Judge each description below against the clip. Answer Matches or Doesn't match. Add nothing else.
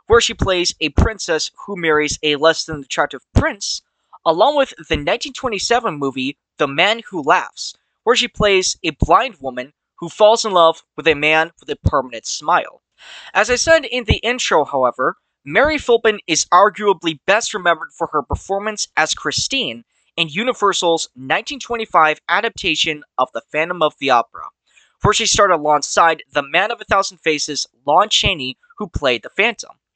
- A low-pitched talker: Doesn't match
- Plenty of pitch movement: Matches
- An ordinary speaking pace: Matches